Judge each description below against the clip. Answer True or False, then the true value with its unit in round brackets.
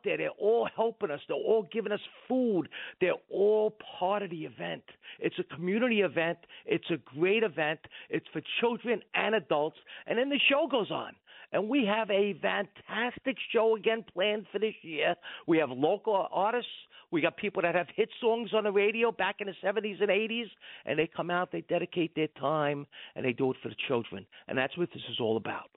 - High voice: True (200 Hz)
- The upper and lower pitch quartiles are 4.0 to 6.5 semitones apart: True (5.2 semitones)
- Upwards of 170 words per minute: True (205 wpm)